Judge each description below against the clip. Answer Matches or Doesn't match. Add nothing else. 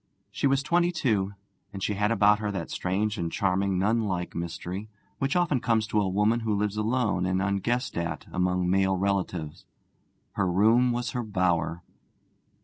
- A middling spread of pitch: Matches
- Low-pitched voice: Matches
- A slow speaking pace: Doesn't match